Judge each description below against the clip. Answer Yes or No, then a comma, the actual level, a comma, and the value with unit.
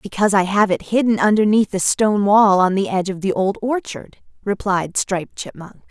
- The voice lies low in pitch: No, high, 200 Hz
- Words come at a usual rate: Yes, average, 195 wpm